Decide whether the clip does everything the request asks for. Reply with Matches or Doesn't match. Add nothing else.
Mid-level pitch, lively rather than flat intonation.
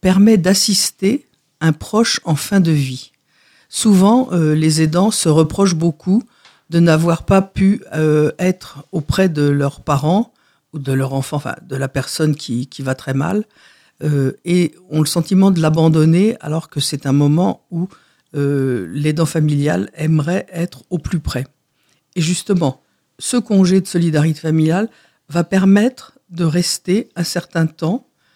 Doesn't match